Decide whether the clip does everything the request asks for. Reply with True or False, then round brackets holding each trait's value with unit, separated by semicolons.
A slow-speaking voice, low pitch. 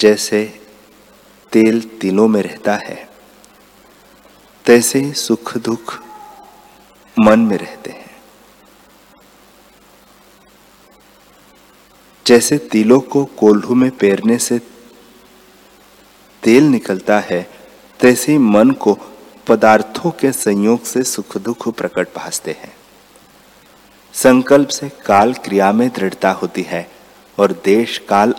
True (95 wpm; 115 Hz)